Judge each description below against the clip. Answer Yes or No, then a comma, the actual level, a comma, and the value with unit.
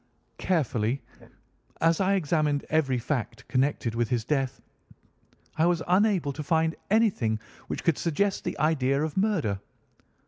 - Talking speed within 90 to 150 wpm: Yes, slow, 135 wpm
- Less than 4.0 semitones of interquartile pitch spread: No, average, 4.9 semitones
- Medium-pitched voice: Yes, medium, 150 Hz